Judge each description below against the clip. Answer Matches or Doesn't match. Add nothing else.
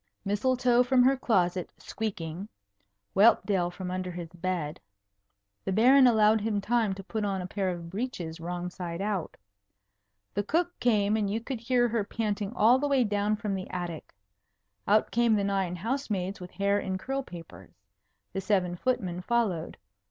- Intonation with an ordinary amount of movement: Matches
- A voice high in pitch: Matches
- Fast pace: Doesn't match